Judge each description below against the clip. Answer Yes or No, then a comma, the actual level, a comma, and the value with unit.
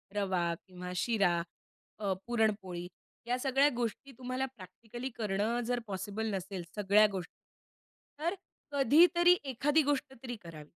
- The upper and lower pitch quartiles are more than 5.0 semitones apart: Yes, wide, 5.5 semitones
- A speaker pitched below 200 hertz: No, high, 220 Hz